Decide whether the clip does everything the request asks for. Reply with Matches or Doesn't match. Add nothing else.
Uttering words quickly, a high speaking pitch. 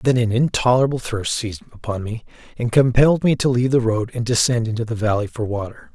Doesn't match